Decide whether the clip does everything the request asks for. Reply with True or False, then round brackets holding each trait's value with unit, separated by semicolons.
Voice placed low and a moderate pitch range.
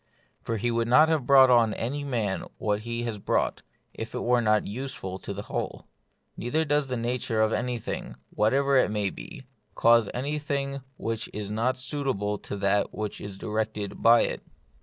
True (115 Hz; 3.9 semitones)